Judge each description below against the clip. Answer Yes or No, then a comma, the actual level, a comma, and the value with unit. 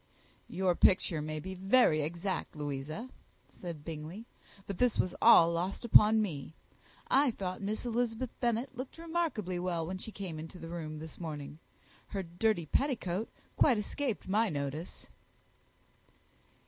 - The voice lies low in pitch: No, medium, 185 Hz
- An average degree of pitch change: No, wide, 5.7 semitones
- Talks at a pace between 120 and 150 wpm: Yes, average, 140 wpm